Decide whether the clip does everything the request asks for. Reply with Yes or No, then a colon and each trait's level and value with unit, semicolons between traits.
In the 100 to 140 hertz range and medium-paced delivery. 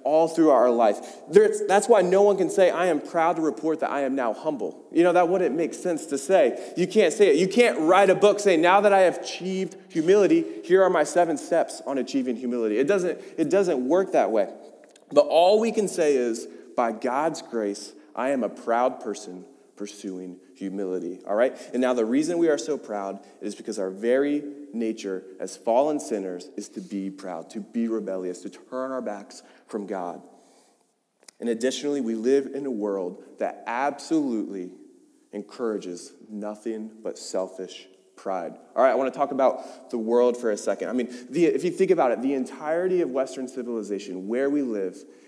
Yes: low, 135 Hz; average, 195 wpm